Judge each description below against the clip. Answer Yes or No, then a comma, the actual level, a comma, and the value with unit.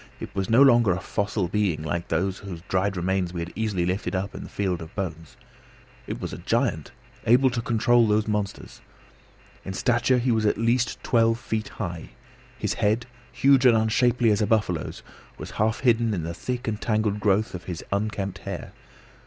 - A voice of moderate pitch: No, low, 105 Hz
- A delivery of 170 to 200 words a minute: Yes, average, 190 wpm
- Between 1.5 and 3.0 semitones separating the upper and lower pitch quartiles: No, average, 3.7 semitones